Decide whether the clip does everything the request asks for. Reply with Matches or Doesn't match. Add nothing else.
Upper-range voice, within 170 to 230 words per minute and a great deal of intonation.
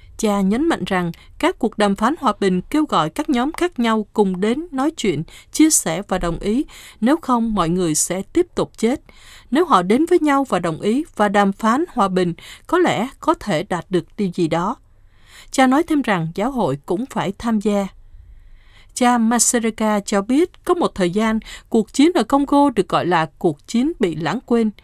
Matches